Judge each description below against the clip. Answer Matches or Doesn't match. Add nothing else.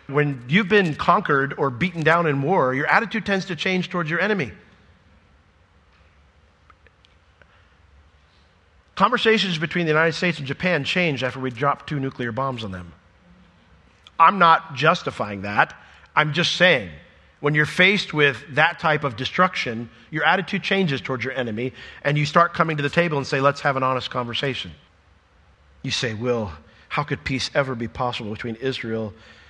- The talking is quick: Doesn't match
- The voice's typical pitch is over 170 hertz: Doesn't match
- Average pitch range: Doesn't match